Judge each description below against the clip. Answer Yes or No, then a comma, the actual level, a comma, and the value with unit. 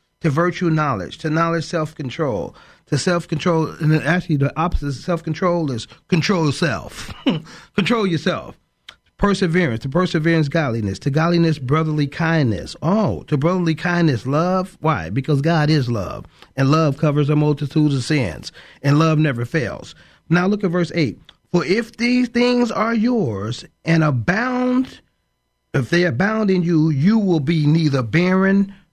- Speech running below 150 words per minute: No, average, 155 wpm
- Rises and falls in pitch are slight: No, average, 3.4 semitones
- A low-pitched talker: No, medium, 160 Hz